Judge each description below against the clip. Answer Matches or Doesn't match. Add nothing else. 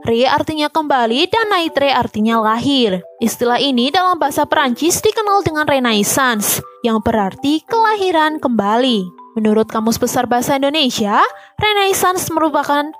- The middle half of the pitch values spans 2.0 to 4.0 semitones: Doesn't match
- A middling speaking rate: Matches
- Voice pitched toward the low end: Doesn't match